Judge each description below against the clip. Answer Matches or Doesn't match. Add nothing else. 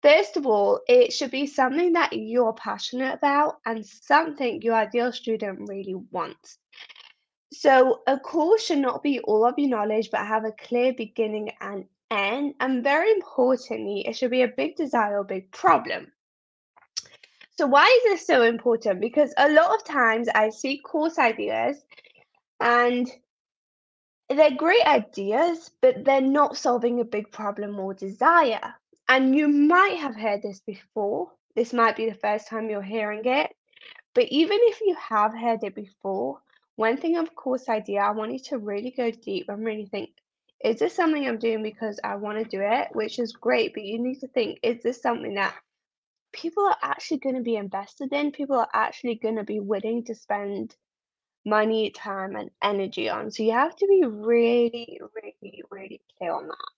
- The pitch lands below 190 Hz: Doesn't match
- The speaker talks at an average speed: Matches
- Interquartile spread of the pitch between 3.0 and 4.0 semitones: Doesn't match